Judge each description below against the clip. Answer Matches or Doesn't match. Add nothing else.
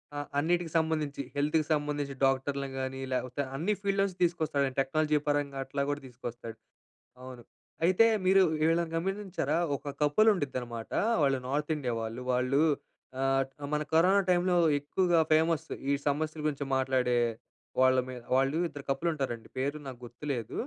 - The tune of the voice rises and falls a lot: Doesn't match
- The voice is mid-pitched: Matches